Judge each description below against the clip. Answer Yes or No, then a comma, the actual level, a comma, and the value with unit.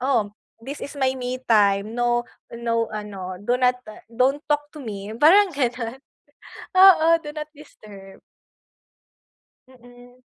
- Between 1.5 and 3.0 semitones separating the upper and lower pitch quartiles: No, average, 4.7 semitones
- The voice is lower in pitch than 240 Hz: No, high, 245 Hz